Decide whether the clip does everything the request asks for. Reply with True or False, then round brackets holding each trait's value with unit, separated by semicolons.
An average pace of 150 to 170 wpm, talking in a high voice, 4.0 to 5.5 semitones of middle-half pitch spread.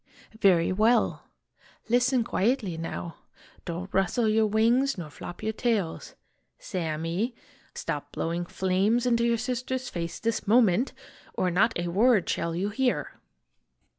False (135 wpm; 215 Hz; 5.2 semitones)